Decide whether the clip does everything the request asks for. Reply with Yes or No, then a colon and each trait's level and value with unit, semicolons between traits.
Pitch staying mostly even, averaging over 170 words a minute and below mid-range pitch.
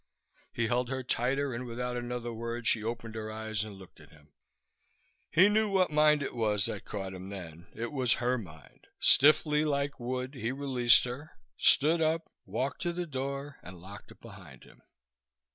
No: average, 4.6 semitones; average, 180 wpm; low, 120 Hz